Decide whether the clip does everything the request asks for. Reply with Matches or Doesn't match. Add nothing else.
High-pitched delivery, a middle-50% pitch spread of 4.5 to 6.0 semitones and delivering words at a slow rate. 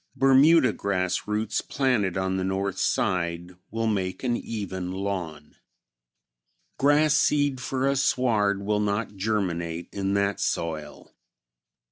Doesn't match